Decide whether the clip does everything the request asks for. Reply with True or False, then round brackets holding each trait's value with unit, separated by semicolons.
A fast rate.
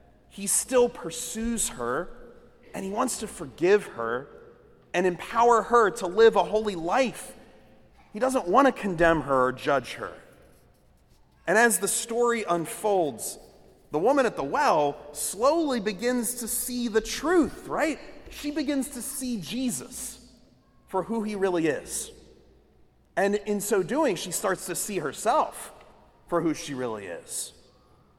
False (145 wpm)